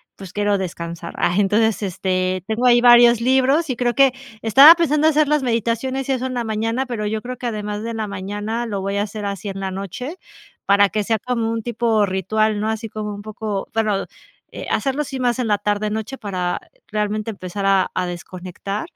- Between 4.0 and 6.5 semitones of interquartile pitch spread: No, average, 3.3 semitones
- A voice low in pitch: No, high, 215 Hz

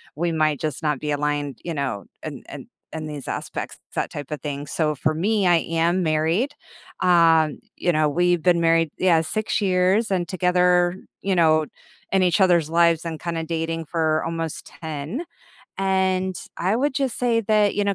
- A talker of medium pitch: Yes, medium, 170 Hz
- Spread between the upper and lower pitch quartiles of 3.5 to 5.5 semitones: No, average, 3.0 semitones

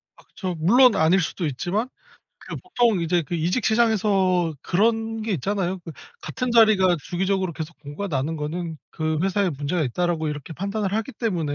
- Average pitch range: Yes, average, 4.8 semitones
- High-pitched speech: No, medium, 180 Hz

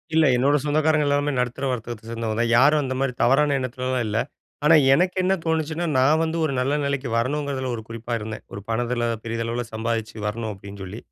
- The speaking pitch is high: No, low, 130 Hz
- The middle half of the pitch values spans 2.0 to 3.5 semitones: No, average, 4.1 semitones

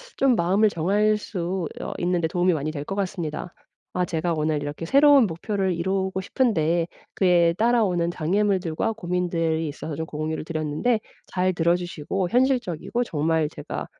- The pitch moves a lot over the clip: No, average, 3.6 semitones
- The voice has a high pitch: No, medium, 175 Hz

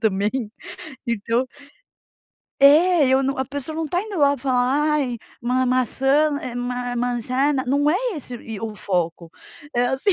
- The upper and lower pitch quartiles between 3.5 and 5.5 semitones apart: No, average, 3.0 semitones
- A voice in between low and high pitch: No, very high, 260 Hz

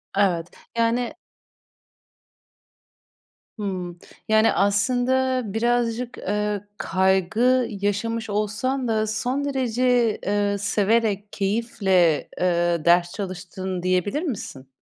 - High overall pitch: Yes, high, 210 Hz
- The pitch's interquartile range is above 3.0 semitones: Yes, average, 3.9 semitones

